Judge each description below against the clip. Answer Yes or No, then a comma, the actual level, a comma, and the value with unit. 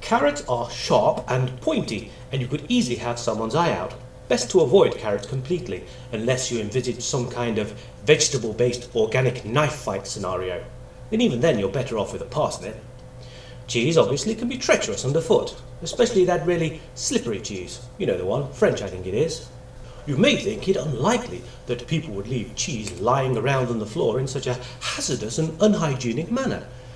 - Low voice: Yes, low, 125 Hz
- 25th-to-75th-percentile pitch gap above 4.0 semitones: No, average, 3.6 semitones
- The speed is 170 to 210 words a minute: Yes, average, 180 wpm